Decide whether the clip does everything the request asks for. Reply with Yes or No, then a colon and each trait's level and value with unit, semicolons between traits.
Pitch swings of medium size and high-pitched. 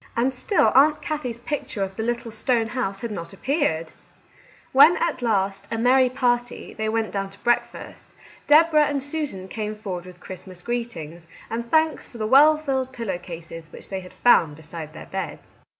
No: wide, 5.7 semitones; high, 230 Hz